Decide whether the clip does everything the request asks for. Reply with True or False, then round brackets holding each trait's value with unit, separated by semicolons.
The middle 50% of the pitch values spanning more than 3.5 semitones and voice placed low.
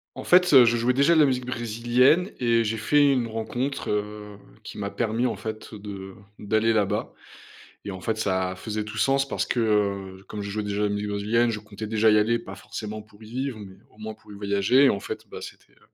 False (2.6 semitones; 110 Hz)